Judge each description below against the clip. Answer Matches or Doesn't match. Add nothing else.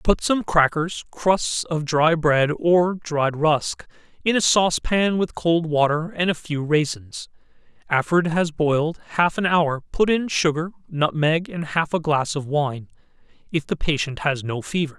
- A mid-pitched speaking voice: Matches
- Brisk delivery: Doesn't match